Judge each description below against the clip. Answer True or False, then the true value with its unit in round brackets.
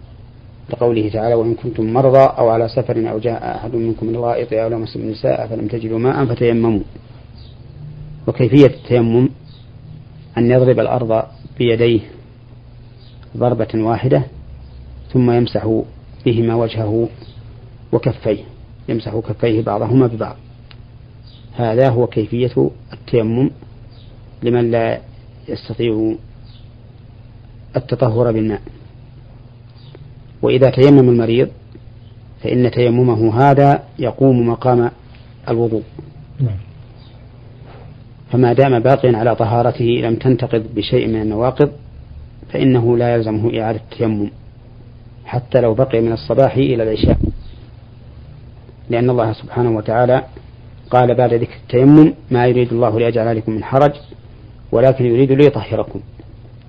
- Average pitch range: False (1.5 semitones)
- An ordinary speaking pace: True (100 wpm)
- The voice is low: True (120 Hz)